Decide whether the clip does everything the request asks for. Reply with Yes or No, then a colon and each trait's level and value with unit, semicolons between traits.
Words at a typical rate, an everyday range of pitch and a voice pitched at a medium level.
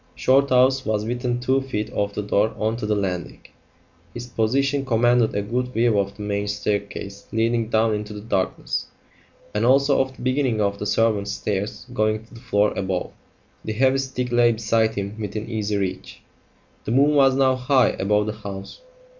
No: average, 180 wpm; average, 3.4 semitones; low, 110 Hz